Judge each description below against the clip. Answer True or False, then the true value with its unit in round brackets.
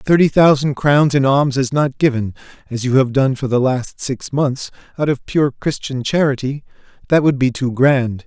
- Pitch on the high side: False (135 Hz)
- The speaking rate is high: False (195 wpm)